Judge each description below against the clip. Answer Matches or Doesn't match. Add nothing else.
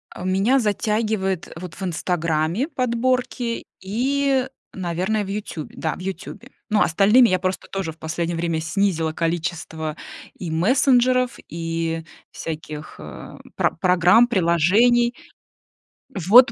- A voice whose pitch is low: Doesn't match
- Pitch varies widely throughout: Matches